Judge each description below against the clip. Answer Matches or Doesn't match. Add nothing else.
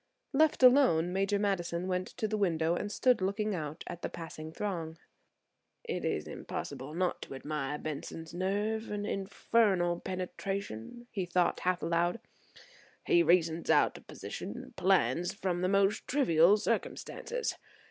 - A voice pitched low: Doesn't match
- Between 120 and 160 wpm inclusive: Matches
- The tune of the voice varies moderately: Matches